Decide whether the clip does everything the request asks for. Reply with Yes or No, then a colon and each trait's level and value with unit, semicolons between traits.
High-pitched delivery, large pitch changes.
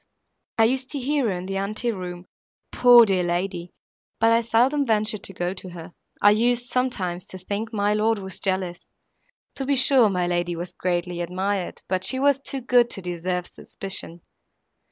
No: high, 200 Hz; average, 5.0 semitones